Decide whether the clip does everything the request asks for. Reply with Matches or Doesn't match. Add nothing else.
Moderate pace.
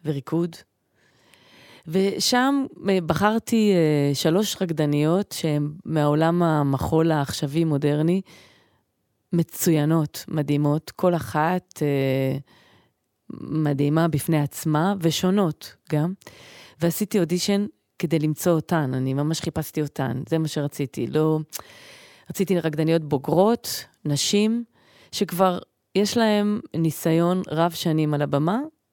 Doesn't match